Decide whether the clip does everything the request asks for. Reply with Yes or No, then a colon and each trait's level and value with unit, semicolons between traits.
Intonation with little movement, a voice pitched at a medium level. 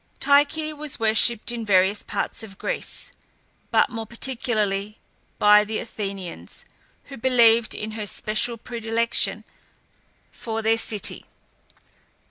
No: narrow, 2.2 semitones; high, 225 Hz